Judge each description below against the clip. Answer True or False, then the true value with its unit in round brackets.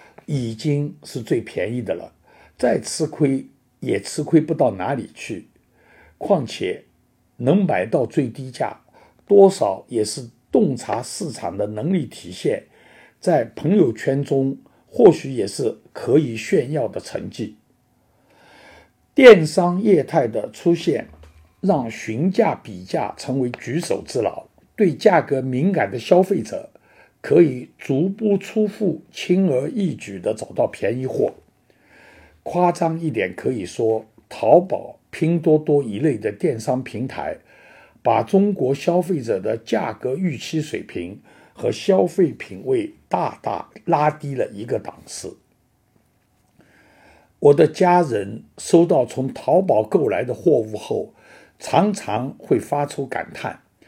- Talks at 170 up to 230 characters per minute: True (185 characters per minute)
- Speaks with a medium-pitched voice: True (155 Hz)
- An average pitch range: False (5.9 semitones)